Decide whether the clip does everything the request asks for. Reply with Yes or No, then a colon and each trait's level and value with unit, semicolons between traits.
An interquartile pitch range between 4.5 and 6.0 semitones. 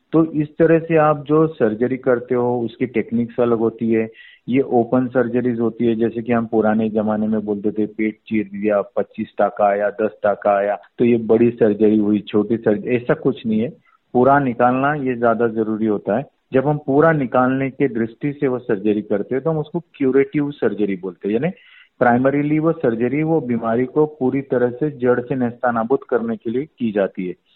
No: average, 3.9 semitones